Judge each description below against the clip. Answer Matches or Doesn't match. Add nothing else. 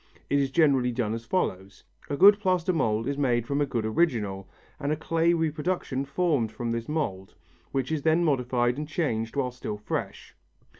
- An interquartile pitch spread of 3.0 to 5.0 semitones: Doesn't match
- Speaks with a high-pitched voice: Doesn't match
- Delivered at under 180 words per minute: Doesn't match